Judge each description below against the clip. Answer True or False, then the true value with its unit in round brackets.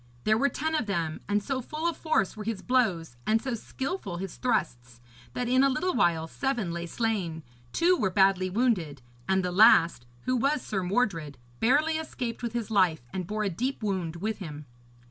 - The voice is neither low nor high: False (210 Hz)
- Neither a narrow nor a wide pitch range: False (6.7 semitones)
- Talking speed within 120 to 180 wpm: False (195 wpm)